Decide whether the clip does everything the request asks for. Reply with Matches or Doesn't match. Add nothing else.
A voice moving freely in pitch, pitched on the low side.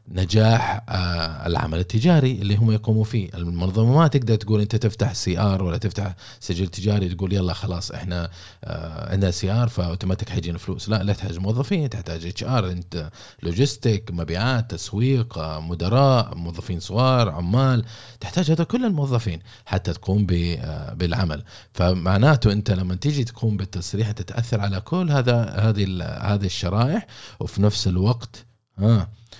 Doesn't match